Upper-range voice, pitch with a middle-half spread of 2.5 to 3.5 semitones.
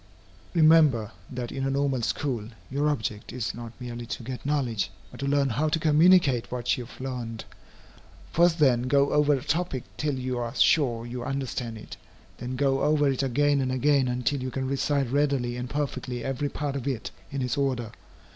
No: low, 135 Hz; average, 2.8 semitones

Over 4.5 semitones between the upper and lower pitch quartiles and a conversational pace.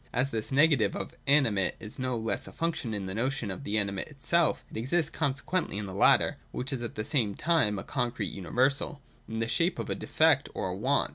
No: average, 5.0 semitones; fast, 220 wpm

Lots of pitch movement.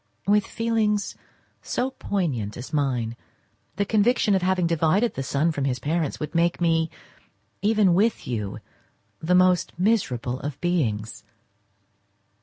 Yes: wide, 6.7 semitones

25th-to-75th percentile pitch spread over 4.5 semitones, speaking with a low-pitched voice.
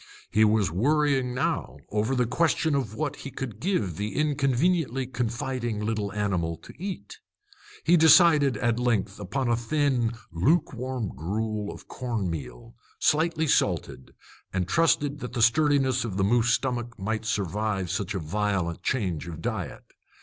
Yes: average, 5.1 semitones; low, 115 Hz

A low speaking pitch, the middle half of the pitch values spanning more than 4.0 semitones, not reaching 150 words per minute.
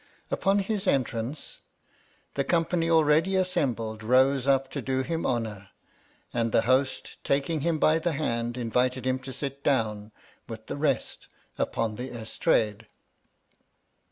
Yes: low, 130 Hz; average, 5.1 semitones; average, 140 wpm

